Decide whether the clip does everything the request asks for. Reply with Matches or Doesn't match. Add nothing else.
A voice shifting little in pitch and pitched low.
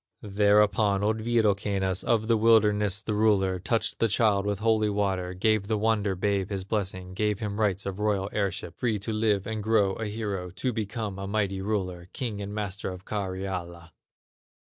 Matches